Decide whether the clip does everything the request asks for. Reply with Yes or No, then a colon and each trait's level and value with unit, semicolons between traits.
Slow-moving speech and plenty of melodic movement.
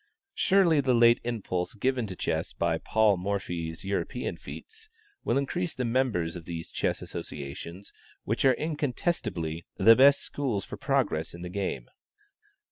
No: average, 145 wpm; wide, 7.5 semitones